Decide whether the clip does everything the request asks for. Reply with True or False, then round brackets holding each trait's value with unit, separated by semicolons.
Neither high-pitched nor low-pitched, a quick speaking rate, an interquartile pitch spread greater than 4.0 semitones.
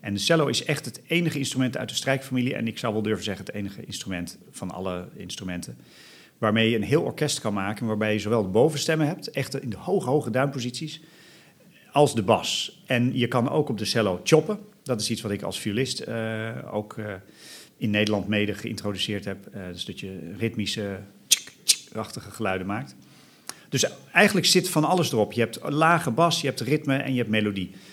False (115 Hz; 205 wpm; 5.6 semitones)